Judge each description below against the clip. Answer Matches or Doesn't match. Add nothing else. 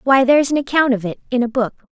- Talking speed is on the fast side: Matches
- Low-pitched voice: Doesn't match